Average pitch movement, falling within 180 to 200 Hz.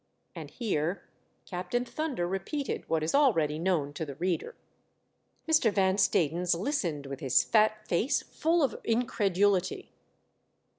No: wide, 6.4 semitones; high, 190 Hz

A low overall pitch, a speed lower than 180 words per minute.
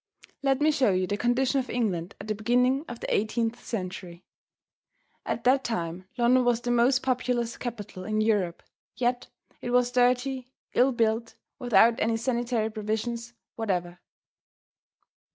No: high, 235 Hz; average, 145 wpm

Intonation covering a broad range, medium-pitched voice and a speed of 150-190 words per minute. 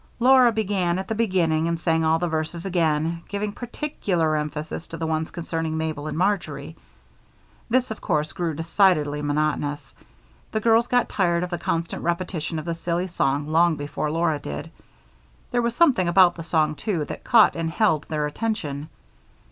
No: average, 3.7 semitones; medium, 170 Hz; average, 170 wpm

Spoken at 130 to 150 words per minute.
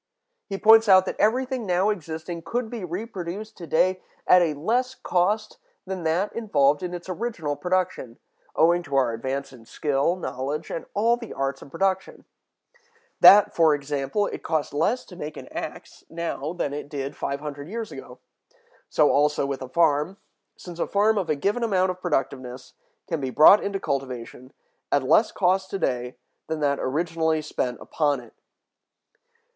No: average, 170 wpm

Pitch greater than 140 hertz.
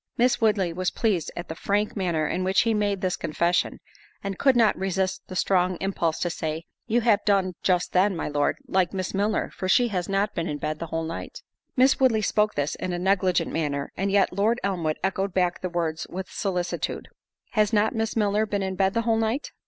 Yes: high, 190 Hz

